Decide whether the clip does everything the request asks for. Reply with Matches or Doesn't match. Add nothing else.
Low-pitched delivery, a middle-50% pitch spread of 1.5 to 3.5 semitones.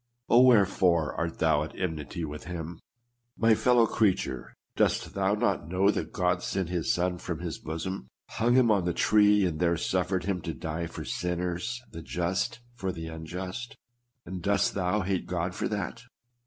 Matches